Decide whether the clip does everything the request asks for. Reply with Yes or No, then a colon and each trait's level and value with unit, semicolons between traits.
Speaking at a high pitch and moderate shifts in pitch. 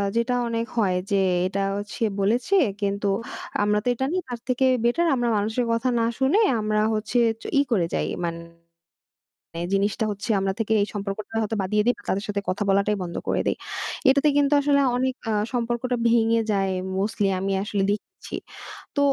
Yes: high, 220 Hz; average, 3.6 semitones